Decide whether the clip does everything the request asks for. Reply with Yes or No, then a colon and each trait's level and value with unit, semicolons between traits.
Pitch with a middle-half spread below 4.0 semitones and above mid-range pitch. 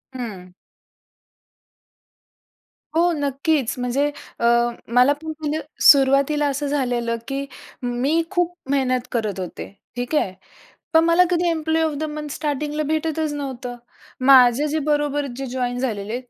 Yes: average, 3.6 semitones; very high, 280 Hz